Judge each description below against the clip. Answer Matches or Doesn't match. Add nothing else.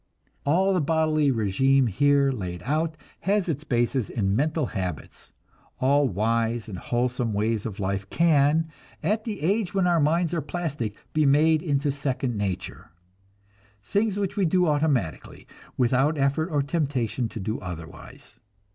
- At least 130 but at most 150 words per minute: Matches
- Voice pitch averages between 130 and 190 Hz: Matches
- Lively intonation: Matches